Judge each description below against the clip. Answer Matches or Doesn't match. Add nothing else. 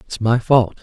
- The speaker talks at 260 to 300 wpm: Doesn't match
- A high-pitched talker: Doesn't match